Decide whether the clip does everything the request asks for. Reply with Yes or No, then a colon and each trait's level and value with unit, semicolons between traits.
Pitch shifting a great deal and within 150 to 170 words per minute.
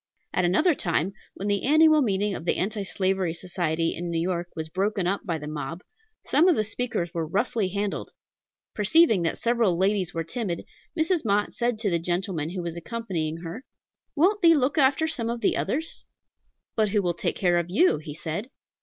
No: wide, 5.7 semitones; average, 195 wpm